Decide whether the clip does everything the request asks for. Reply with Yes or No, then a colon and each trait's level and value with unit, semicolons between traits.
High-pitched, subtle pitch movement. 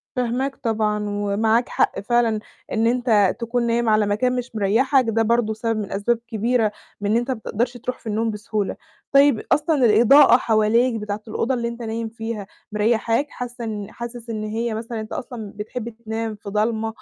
Yes: high, 225 Hz; narrow, 2.0 semitones